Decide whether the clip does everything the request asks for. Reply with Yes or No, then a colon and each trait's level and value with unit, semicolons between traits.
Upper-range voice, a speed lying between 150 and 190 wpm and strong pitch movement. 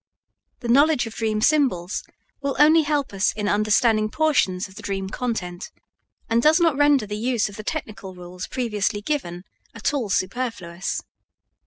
Yes: high, 220 Hz; average, 160 wpm; wide, 5.9 semitones